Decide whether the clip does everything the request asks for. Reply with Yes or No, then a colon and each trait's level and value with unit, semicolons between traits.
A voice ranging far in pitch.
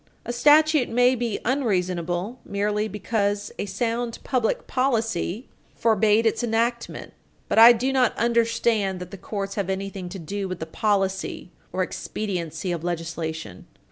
No: average, 4.1 semitones